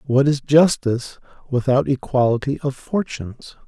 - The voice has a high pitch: No, low, 130 Hz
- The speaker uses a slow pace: Yes, slow, 115 wpm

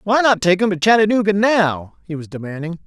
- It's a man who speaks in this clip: Yes, male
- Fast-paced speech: Yes, fast, 210 wpm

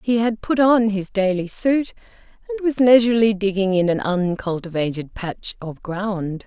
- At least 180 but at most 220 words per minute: No, average, 160 wpm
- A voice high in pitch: Yes, high, 205 Hz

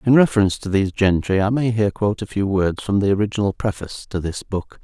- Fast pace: Yes, fast, 235 wpm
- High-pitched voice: No, low, 100 Hz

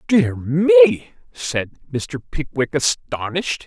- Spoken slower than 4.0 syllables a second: Yes, 3.7 syllables/s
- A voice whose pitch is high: No, medium, 150 Hz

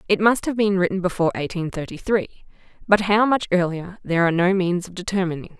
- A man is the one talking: No, female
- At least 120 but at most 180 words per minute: No, fast, 205 wpm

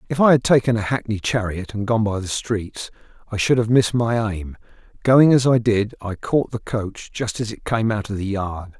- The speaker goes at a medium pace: No, fast, 230 wpm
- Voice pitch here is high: No, low, 110 Hz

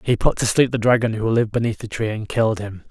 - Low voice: Yes, low, 110 Hz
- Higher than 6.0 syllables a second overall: Yes, 6.5 syllables/s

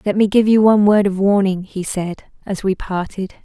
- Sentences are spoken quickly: Yes, fast, 225 wpm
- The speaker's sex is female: Yes, female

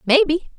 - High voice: Yes, very high, 320 Hz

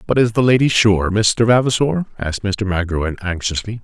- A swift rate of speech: No, average, 170 wpm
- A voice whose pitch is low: Yes, low, 105 Hz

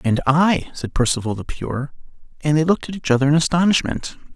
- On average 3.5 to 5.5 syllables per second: No, 5.9 syllables/s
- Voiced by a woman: No, male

